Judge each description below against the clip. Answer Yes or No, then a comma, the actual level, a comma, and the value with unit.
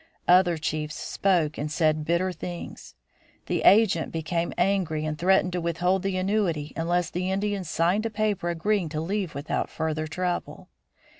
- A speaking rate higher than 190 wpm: No, average, 155 wpm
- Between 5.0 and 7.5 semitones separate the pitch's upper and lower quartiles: No, average, 3.2 semitones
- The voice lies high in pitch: No, medium, 175 Hz